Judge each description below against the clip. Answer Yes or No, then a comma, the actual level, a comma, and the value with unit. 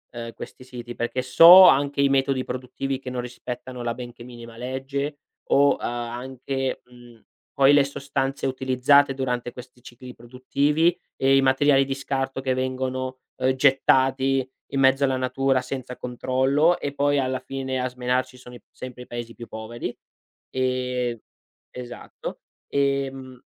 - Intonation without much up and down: Yes, narrow, 1.5 semitones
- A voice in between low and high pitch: No, low, 130 Hz